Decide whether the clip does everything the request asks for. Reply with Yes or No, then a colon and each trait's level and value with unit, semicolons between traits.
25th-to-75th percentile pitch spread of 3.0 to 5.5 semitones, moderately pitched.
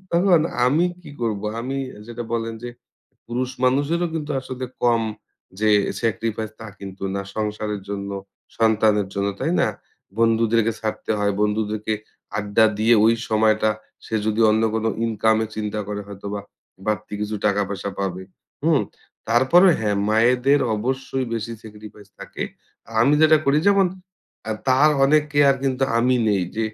No: average, 3.4 semitones; low, 110 Hz